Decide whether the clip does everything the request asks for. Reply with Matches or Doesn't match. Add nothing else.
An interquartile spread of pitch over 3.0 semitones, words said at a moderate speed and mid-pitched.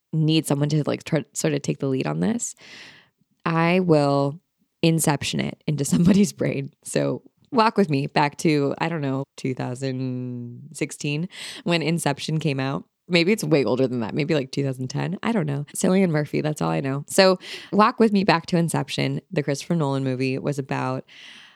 Matches